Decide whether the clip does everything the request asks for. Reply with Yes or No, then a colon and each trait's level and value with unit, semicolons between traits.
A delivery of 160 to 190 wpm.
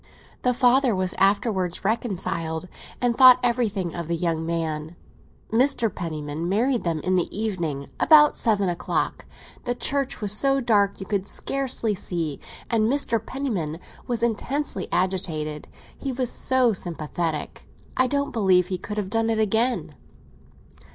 No: average, 145 wpm